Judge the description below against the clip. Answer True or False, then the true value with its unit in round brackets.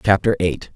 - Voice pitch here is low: True (95 Hz)